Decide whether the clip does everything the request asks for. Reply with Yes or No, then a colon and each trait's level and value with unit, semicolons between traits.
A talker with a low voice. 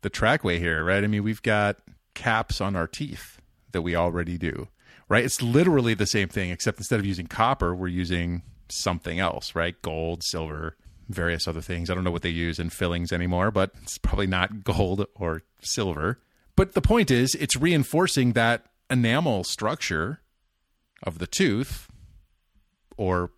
Yes: very low, 95 Hz